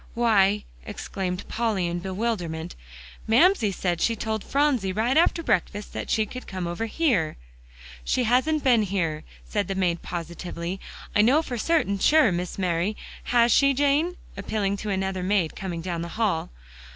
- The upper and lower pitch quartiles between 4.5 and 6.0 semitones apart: Yes, average, 4.8 semitones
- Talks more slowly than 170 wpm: Yes, average, 160 wpm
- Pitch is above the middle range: Yes, high, 205 Hz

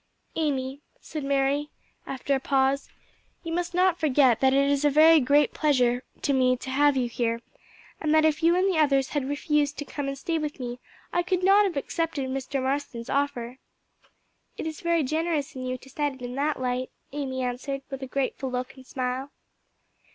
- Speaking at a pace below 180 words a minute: No, average, 195 wpm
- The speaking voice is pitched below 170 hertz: No, very high, 275 Hz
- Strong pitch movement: No, average, 2.8 semitones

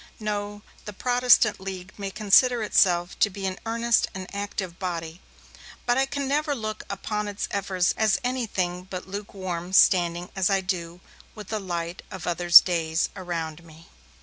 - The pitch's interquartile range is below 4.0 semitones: Yes, average, 3.2 semitones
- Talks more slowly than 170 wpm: Yes, average, 160 wpm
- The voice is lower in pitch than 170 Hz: No, high, 190 Hz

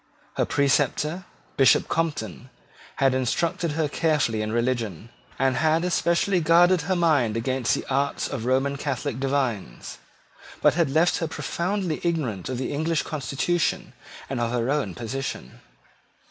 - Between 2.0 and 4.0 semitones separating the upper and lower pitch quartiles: No, average, 4.8 semitones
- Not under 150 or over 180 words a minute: No, average, 140 wpm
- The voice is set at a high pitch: No, medium, 140 Hz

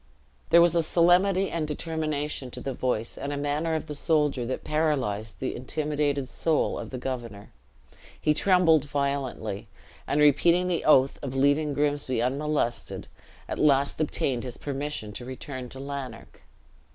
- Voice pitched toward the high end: No, medium, 145 Hz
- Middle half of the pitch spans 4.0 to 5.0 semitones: No, average, 2.9 semitones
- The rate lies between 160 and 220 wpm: No, average, 150 wpm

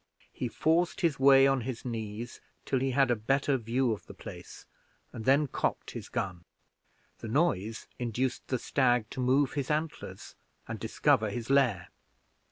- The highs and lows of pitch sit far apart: No, average, 3.2 semitones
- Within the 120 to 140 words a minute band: No, average, 165 wpm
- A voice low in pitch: Yes, low, 125 Hz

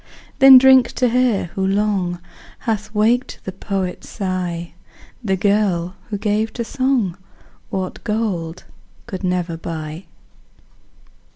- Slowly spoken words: Yes, slow, 115 wpm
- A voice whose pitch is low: No, high, 195 Hz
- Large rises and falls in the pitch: No, average, 3.8 semitones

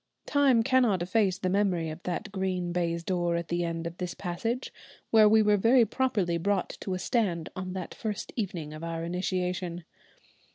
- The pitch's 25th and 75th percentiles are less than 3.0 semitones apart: No, average, 3.6 semitones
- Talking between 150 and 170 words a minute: No, average, 180 wpm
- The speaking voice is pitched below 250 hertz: Yes, medium, 185 Hz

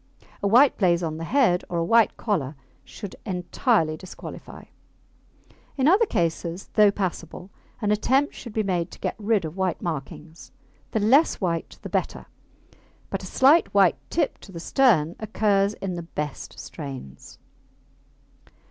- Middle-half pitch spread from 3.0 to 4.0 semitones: No, average, 4.8 semitones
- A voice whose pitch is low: No, high, 190 Hz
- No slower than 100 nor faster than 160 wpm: Yes, average, 150 wpm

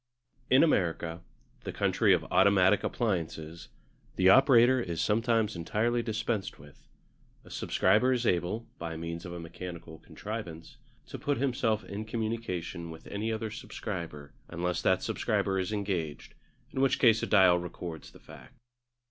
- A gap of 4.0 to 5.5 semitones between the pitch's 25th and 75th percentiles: Yes, average, 5.1 semitones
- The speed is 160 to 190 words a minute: No, average, 145 wpm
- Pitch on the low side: Yes, very low, 95 Hz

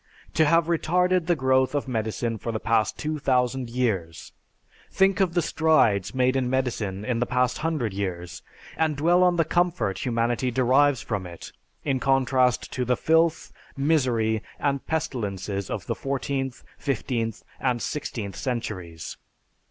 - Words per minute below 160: Yes, average, 145 wpm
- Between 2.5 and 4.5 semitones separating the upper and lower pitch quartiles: No, average, 4.9 semitones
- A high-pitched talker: No, low, 130 Hz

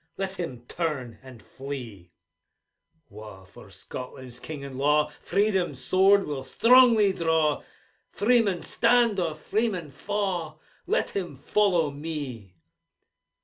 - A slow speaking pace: Yes, slow, 110 wpm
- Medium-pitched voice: Yes, medium, 160 Hz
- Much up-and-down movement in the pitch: Yes, wide, 6.8 semitones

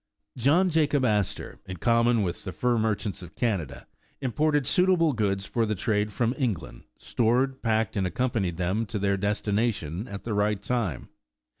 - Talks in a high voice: No, low, 110 Hz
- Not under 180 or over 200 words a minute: No, average, 160 wpm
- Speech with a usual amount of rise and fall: Yes, average, 4.0 semitones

